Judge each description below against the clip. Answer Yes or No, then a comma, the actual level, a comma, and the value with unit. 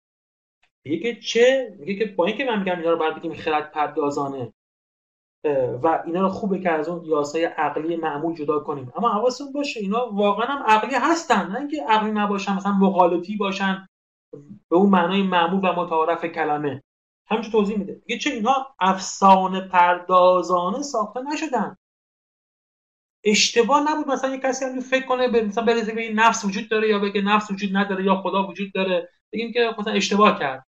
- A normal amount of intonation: Yes, average, 4.9 semitones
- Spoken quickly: Yes, fast, 170 wpm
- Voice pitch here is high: Yes, high, 200 Hz